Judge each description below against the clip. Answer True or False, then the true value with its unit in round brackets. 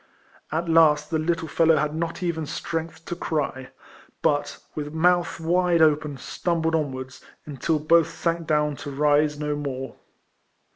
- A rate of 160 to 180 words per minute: False (150 wpm)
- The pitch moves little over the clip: True (2.0 semitones)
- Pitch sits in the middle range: True (155 Hz)